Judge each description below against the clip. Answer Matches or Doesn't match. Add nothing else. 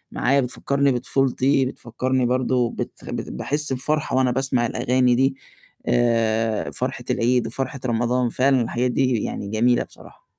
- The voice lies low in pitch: Matches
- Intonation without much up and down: Matches